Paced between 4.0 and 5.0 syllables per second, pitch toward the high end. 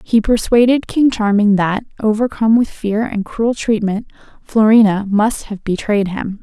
Yes: 4.5 syllables/s; high, 215 Hz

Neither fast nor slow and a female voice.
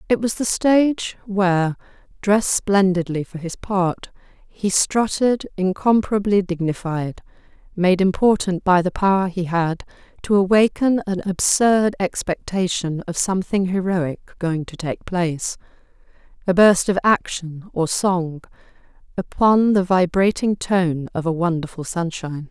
No: slow, 120 wpm; female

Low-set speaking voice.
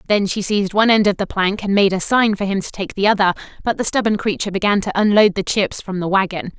No: high, 200 Hz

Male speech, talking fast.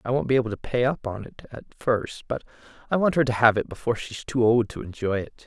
Yes: male; fast, 285 wpm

